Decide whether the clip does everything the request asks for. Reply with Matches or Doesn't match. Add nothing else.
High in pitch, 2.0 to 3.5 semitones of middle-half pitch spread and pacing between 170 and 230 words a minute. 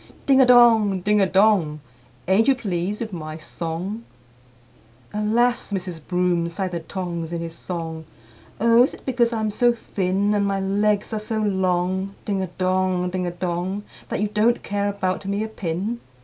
Matches